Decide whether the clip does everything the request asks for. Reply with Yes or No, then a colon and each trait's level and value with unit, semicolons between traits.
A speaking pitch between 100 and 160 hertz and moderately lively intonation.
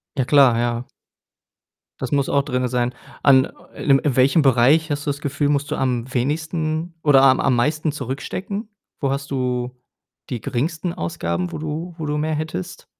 Yes: medium, 140 Hz; average, 3.4 semitones